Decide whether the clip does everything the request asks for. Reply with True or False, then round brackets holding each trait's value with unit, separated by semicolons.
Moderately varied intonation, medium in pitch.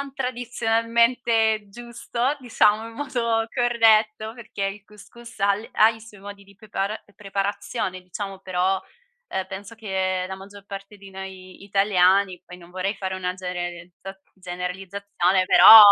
False (3.0 semitones; 200 Hz)